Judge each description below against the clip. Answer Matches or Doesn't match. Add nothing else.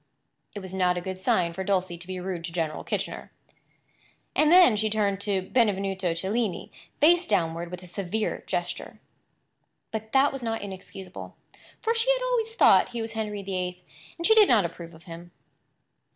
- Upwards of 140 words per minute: Matches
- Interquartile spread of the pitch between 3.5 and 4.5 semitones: Matches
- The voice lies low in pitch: Doesn't match